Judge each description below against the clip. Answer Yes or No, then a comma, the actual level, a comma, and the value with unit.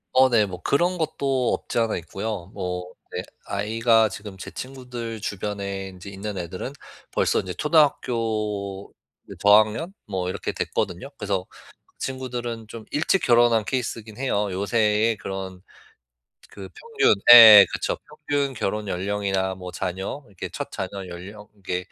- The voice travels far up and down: No, average, 3.7 semitones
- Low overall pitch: Yes, low, 105 Hz